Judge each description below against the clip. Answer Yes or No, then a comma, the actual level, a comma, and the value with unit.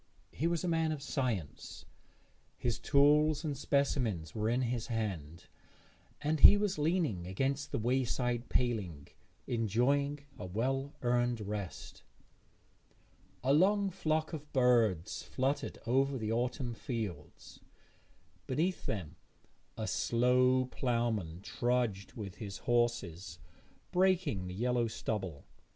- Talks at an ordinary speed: No, slow, 115 wpm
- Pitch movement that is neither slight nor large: Yes, average, 5.0 semitones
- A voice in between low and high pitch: No, low, 125 Hz